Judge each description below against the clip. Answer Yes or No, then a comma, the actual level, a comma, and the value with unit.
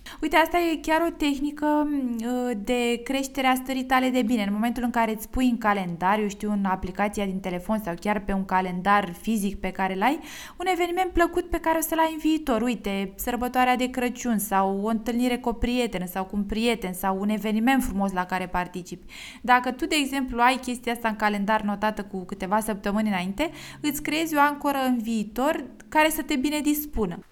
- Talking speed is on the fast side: Yes, fast, 200 wpm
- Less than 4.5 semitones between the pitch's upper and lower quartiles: No, wide, 5.6 semitones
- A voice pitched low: No, high, 240 Hz